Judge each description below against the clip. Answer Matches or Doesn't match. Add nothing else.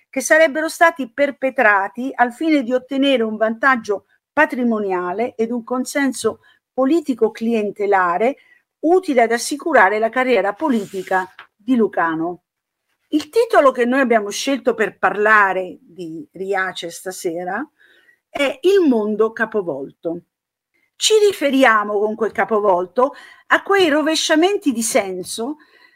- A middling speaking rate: Doesn't match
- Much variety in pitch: Matches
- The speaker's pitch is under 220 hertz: Doesn't match